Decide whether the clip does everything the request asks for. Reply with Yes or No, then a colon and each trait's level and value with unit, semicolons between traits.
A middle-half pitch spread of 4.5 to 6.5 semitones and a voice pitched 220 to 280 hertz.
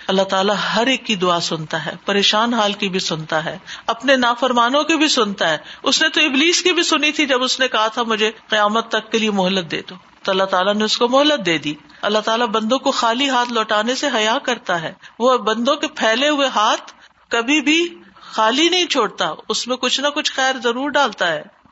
Yes: average, 5.1 semitones; high, 230 Hz